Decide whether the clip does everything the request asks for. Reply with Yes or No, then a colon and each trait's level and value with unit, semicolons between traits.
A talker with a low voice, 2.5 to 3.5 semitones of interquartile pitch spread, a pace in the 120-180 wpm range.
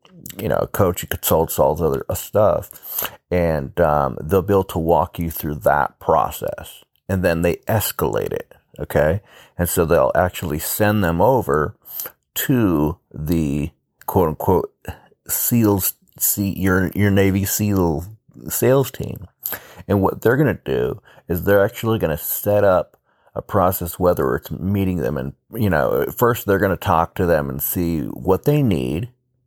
No: very low, 95 Hz; average, 3.9 semitones; average, 165 wpm